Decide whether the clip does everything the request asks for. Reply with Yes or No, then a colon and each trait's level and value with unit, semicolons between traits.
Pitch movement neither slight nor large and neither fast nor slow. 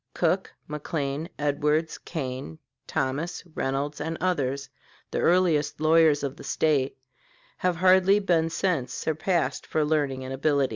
No: average, 3.1 semitones; slow, 130 wpm